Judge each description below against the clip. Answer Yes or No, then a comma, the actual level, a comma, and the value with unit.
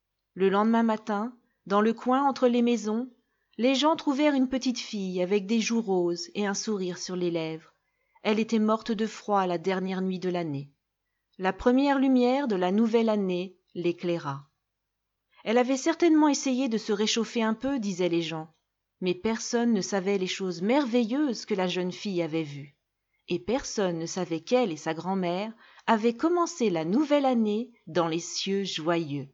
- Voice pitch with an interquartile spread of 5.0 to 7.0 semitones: Yes, wide, 5.5 semitones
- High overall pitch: Yes, high, 205 Hz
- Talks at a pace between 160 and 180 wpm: Yes, average, 175 wpm